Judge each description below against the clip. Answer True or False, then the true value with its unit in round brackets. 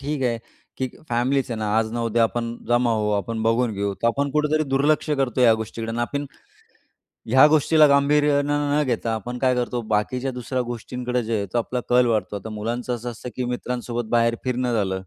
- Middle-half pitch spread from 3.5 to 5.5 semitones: False (2.9 semitones)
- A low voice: True (120 Hz)